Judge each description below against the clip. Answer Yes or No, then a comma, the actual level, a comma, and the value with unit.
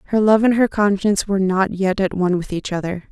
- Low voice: No, high, 195 Hz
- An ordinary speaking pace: No, fast, 250 wpm